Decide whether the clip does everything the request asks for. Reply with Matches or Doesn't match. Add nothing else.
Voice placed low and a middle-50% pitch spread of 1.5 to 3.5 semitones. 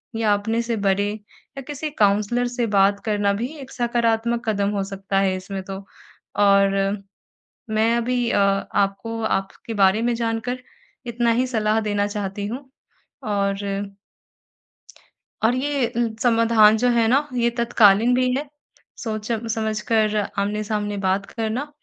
Doesn't match